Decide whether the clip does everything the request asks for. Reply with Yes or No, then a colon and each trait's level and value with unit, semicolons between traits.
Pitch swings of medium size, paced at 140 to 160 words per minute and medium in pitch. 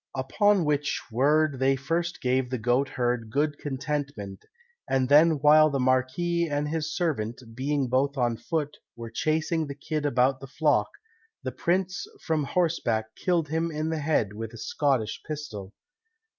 Yes: average, 3.6 semitones; average, 155 wpm; medium, 145 Hz